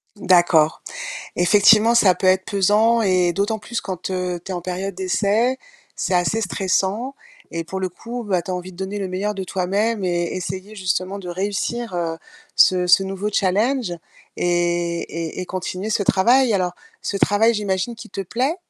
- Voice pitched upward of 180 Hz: Yes, high, 190 Hz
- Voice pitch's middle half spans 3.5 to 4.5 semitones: No, narrow, 2.6 semitones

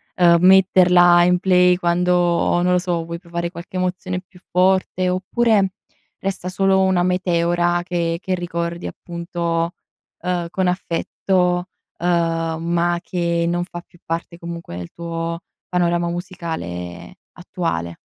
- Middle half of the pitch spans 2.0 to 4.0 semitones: No, narrow, 1.2 semitones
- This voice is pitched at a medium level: Yes, medium, 175 Hz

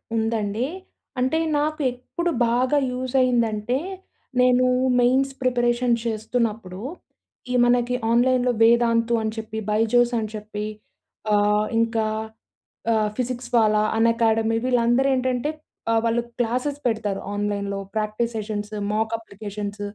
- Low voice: No, high, 230 Hz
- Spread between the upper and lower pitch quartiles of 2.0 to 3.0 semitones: Yes, narrow, 2.6 semitones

